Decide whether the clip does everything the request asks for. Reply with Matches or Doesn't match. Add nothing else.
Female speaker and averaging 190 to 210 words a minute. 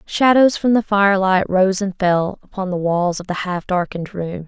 Matches